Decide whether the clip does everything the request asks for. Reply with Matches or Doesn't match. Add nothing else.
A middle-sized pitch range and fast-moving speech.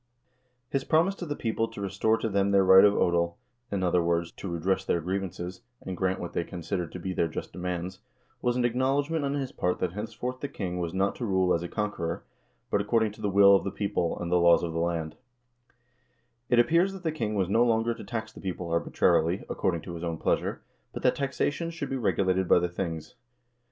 Matches